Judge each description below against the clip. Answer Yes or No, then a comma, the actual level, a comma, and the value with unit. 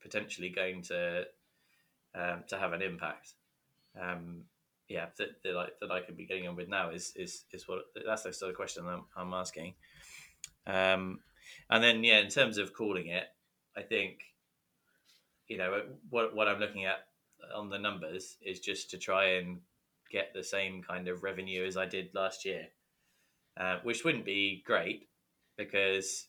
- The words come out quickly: No, average, 175 wpm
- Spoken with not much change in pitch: Yes, narrow, 1.7 semitones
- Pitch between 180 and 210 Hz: No, very low, 95 Hz